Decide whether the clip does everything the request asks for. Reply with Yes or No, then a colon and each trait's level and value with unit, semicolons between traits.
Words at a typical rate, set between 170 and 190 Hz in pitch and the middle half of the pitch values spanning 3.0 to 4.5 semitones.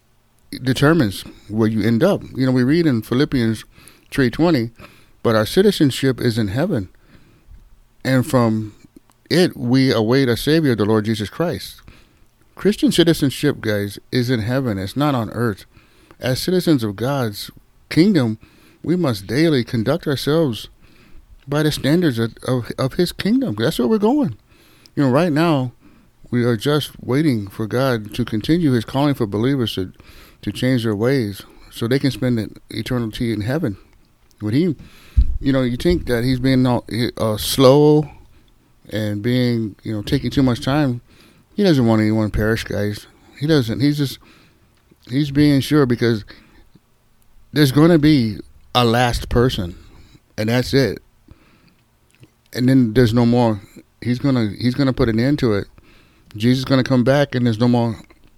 No: average, 160 wpm; low, 125 Hz; average, 4.1 semitones